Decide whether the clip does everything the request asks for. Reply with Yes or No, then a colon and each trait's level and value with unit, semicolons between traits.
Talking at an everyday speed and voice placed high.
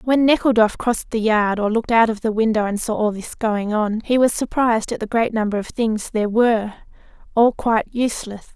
No: fast, 215 wpm; high, 220 Hz